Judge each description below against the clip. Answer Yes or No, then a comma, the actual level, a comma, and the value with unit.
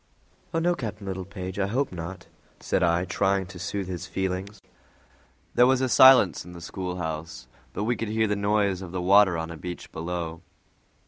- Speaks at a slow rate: No, average, 185 wpm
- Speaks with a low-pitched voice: Yes, very low, 95 Hz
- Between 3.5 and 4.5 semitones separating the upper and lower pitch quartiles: No, average, 2.8 semitones